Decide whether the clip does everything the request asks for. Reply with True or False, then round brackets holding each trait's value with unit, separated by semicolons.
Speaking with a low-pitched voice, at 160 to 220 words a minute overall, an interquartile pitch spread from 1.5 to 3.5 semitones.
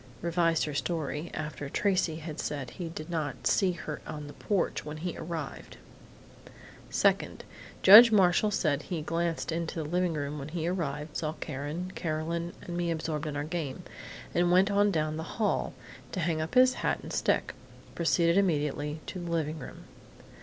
False (165 Hz; 175 wpm; 2.5 semitones)